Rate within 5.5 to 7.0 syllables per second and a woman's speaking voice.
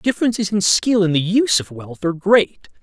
No: 5.6 syllables/s; male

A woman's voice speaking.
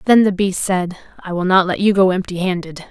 Yes: female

